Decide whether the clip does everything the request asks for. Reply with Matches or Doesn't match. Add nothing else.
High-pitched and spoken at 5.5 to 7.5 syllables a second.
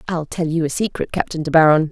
Doesn't match